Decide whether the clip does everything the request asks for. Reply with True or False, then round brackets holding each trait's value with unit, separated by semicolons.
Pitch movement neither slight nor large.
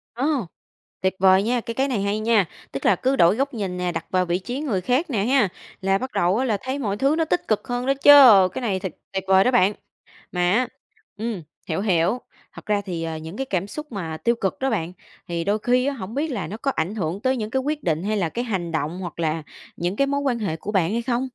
False (5.7 semitones)